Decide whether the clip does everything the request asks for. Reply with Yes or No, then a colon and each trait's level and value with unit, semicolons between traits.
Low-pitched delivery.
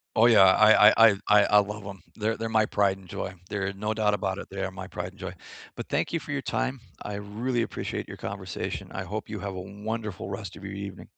Yes: low, 105 Hz